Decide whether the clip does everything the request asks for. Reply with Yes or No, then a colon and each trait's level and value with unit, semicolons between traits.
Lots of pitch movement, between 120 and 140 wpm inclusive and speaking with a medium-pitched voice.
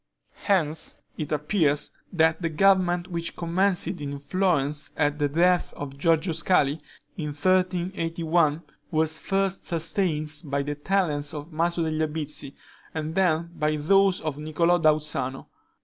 No: average, 2.9 semitones; slow, 135 wpm; medium, 160 Hz